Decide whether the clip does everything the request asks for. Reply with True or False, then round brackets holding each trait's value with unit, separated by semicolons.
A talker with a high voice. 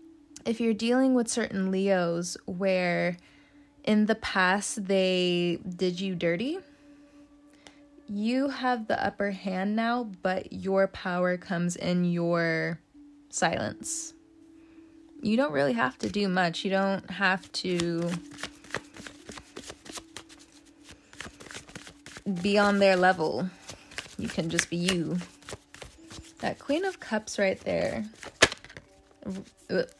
True (200 Hz)